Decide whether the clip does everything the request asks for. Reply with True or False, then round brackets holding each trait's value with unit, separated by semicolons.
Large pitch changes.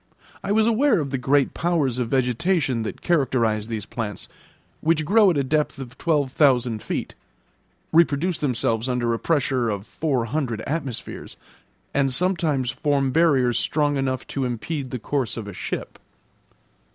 False (4.4 semitones)